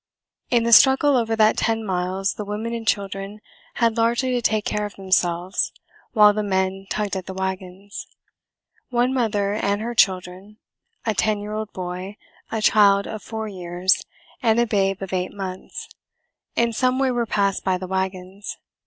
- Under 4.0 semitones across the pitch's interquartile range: Yes, average, 2.9 semitones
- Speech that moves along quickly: No, average, 170 wpm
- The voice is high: Yes, high, 205 Hz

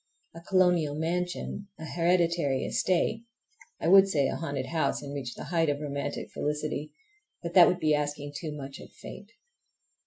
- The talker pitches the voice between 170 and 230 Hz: No, medium, 160 Hz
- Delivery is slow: No, average, 160 wpm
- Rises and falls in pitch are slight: No, average, 3.5 semitones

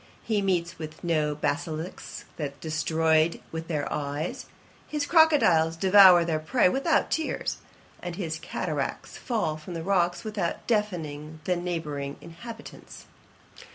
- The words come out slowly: Yes, slow, 125 wpm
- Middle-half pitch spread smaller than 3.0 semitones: No, average, 4.0 semitones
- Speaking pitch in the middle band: Yes, medium, 170 Hz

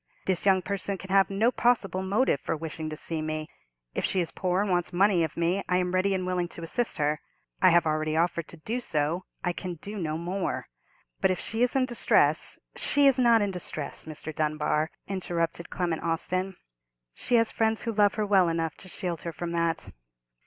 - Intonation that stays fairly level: No, average, 3.3 semitones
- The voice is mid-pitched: Yes, medium, 180 Hz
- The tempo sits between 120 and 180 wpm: No, fast, 205 wpm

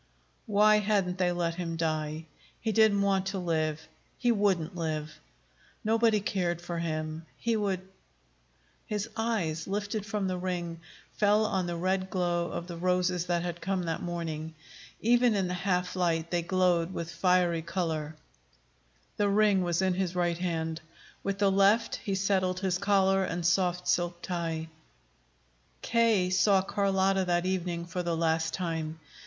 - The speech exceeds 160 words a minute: No, average, 155 wpm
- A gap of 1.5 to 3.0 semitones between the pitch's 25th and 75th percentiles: Yes, narrow, 2.6 semitones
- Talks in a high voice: No, medium, 180 Hz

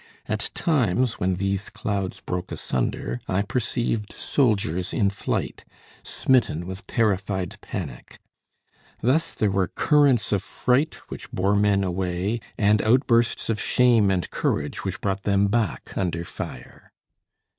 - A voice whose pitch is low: Yes, low, 100 Hz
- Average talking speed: No, slow, 130 wpm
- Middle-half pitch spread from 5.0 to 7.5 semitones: No, average, 4.0 semitones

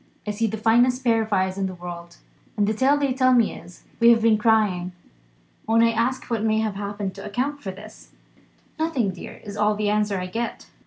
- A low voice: No, high, 215 Hz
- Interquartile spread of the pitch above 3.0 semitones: No, average, 2.7 semitones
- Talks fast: Yes, fast, 220 wpm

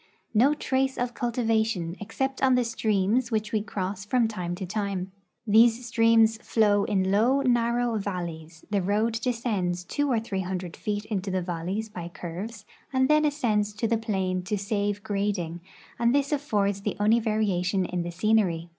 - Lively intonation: No, average, 3.6 semitones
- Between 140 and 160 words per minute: No, average, 170 wpm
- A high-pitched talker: Yes, high, 210 Hz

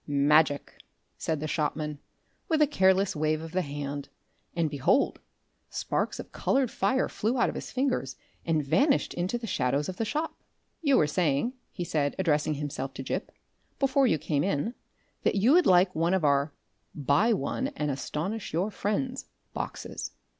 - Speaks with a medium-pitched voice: Yes, medium, 165 Hz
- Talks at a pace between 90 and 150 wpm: No, average, 170 wpm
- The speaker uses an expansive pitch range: Yes, wide, 7.6 semitones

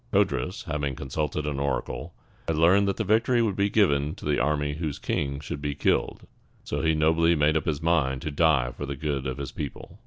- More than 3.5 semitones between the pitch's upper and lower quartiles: No, average, 2.9 semitones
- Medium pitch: No, very low, 75 Hz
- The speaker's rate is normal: No, fast, 215 wpm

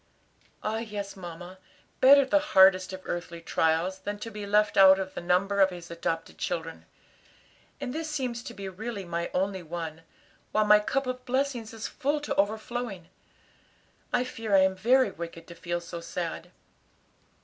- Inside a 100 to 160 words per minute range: No, average, 170 wpm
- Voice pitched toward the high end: Yes, high, 195 Hz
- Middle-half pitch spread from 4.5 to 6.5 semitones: Yes, average, 4.8 semitones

